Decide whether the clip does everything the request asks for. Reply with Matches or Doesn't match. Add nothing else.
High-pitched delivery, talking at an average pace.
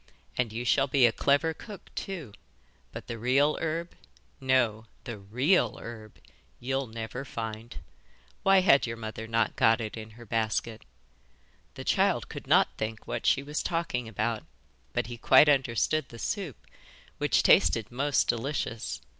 Doesn't match